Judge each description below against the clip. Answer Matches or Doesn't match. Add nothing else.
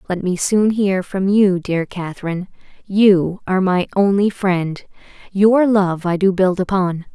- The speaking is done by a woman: Matches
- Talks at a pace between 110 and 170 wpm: Matches